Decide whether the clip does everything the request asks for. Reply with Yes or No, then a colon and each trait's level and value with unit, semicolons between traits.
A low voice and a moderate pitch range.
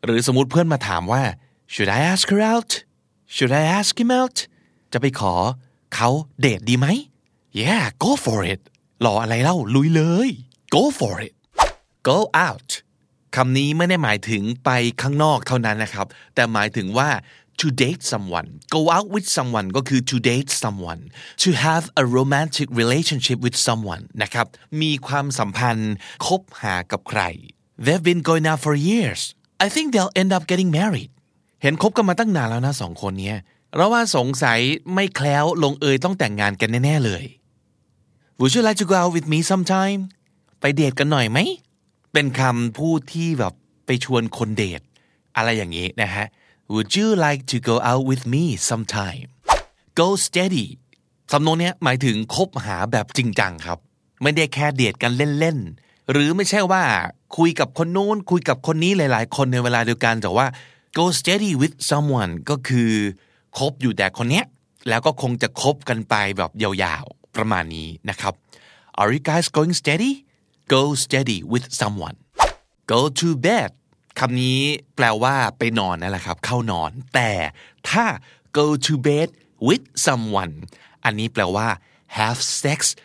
No: low, 130 Hz; wide, 6.1 semitones